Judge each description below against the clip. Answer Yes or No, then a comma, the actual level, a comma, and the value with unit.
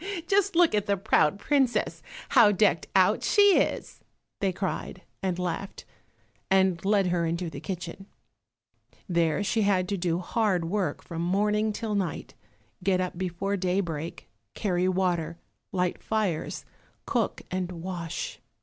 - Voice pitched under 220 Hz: Yes, medium, 185 Hz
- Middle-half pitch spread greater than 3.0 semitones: No, average, 2.7 semitones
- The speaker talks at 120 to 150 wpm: Yes, average, 140 wpm